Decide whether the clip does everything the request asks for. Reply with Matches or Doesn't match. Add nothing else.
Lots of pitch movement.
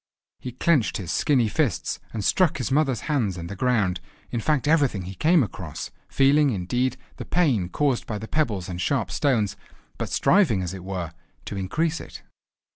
Matches